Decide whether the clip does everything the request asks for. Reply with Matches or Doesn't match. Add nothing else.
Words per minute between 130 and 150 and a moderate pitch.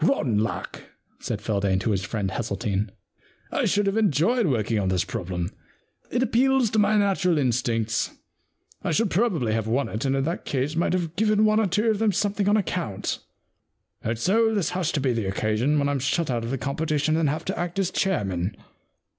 Doesn't match